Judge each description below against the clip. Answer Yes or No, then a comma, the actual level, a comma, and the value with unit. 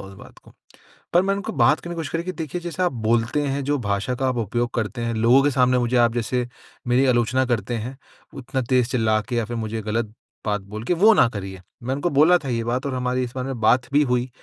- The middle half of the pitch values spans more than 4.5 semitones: No, average, 2.9 semitones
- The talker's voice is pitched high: No, low, 125 Hz